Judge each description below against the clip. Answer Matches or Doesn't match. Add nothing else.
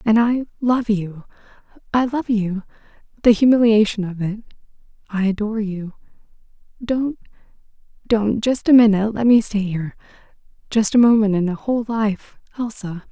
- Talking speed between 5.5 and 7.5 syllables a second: Doesn't match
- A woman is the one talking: Matches